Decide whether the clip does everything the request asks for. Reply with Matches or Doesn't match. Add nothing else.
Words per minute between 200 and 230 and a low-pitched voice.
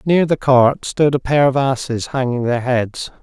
Matches